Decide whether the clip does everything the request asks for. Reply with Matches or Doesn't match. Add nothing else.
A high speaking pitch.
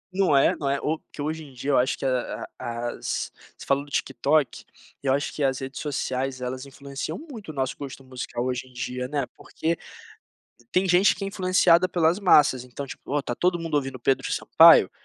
Doesn't match